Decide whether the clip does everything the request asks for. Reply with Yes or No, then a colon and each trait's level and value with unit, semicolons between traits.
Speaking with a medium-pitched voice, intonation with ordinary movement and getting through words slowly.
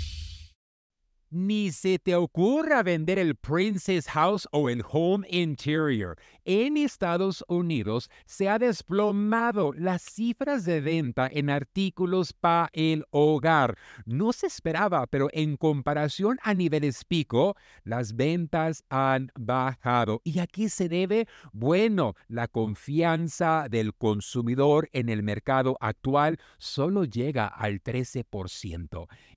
No: medium, 155 Hz; wide, 7.0 semitones; slow, 115 wpm